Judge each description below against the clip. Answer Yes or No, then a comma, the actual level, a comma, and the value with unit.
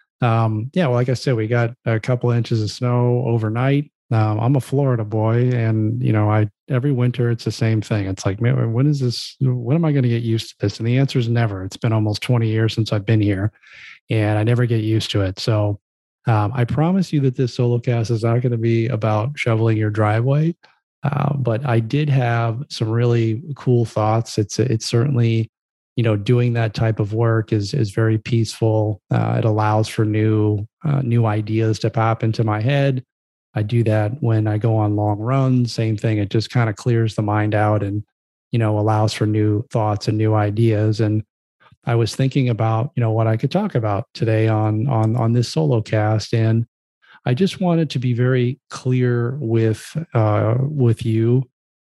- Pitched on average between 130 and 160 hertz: No, low, 115 Hz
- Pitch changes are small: Yes, narrow, 2.3 semitones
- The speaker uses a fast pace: Yes, fast, 210 wpm